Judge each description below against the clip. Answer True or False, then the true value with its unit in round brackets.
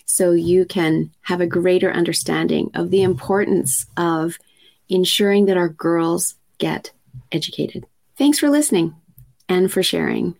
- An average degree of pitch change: False (2.2 semitones)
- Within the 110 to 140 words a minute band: True (135 wpm)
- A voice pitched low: False (175 Hz)